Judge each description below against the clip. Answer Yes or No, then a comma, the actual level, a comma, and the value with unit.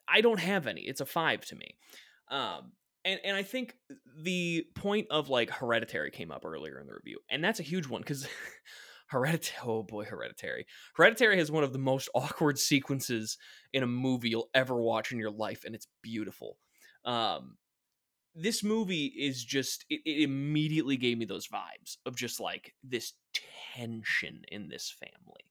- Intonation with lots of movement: Yes, wide, 7.2 semitones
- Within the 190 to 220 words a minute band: No, average, 175 wpm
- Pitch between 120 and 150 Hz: Yes, medium, 140 Hz